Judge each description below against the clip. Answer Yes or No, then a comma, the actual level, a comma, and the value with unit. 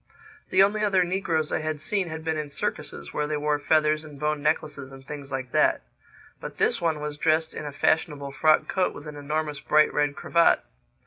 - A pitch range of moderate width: No, narrow, 1.5 semitones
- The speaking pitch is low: No, medium, 150 Hz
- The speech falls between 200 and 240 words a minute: Yes, fast, 205 wpm